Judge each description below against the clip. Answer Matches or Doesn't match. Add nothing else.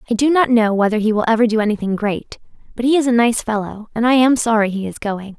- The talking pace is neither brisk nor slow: Doesn't match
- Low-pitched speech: Doesn't match